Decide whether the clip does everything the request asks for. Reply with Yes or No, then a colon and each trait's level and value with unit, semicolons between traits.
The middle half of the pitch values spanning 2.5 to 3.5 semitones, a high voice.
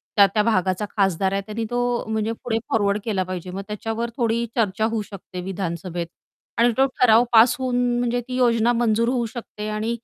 Yes: average, 3.0 semitones; high, 220 Hz